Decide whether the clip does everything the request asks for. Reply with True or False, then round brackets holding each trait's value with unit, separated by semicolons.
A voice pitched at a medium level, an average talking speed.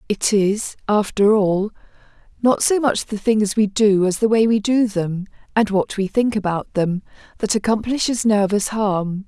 False (210 Hz; 175 wpm)